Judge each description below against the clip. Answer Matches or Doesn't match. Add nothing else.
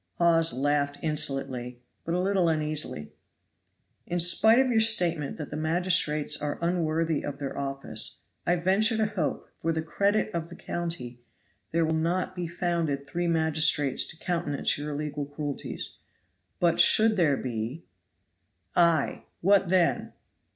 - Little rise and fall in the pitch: Doesn't match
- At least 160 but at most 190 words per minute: Doesn't match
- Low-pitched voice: Doesn't match